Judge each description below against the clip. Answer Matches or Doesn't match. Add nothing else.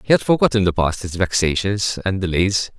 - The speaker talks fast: Doesn't match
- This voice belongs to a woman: Doesn't match